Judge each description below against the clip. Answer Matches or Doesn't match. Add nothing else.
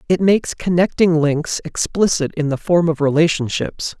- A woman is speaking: Doesn't match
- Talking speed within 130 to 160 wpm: Matches